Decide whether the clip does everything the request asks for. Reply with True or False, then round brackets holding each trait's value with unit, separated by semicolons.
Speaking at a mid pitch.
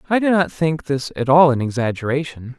True (145 Hz)